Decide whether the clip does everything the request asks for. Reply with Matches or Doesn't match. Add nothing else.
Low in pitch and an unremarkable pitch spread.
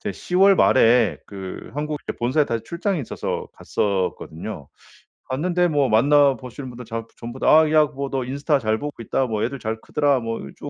Matches